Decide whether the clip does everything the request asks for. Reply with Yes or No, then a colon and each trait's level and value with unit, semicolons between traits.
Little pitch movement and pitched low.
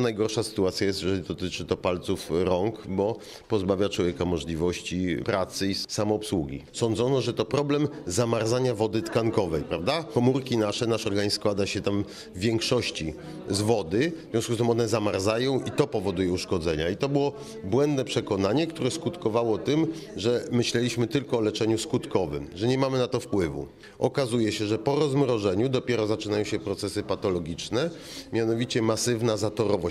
No: average, 3.7 semitones; low, 110 Hz